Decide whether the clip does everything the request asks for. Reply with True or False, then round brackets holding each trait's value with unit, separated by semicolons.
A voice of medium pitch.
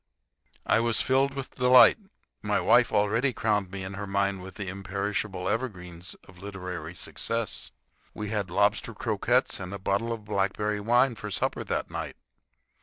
False (100 Hz)